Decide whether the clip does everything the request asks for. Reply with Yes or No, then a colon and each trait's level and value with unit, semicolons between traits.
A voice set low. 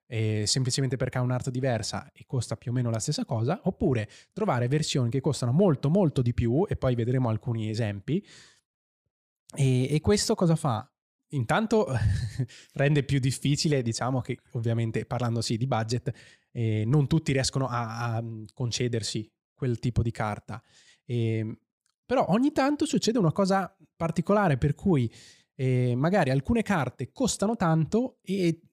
Yes: low, 130 Hz